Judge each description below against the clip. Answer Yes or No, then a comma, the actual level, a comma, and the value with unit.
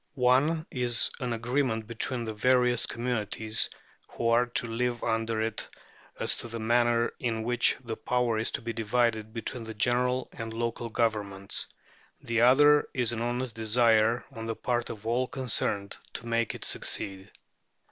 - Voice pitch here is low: Yes, low, 115 Hz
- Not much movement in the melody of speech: Yes, narrow, 1.7 semitones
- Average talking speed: Yes, average, 160 wpm